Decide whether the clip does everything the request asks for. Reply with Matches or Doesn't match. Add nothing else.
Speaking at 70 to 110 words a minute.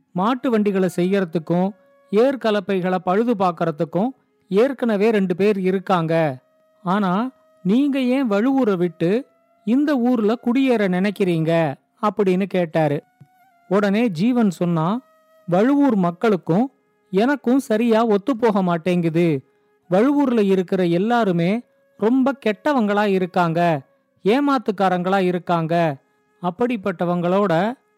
Matches